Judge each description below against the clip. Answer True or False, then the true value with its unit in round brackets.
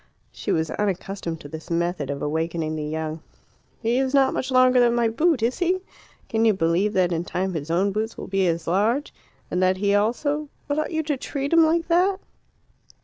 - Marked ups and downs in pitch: True (8.1 semitones)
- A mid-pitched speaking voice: False (205 Hz)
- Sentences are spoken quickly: True (210 wpm)